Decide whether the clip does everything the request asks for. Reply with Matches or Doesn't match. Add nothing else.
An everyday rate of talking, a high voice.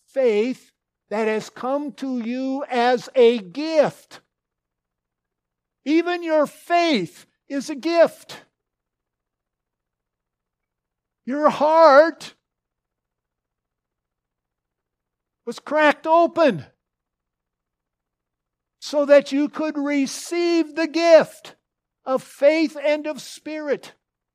Doesn't match